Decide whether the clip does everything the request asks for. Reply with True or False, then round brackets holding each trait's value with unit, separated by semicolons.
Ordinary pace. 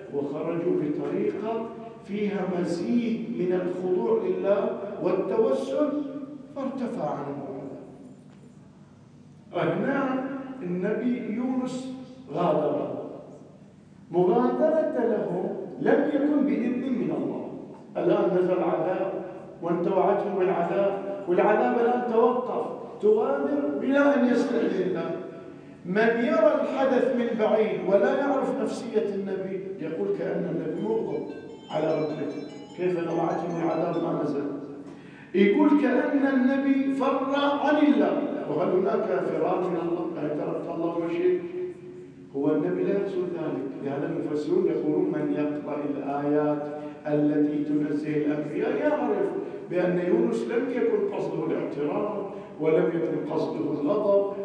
True (105 wpm)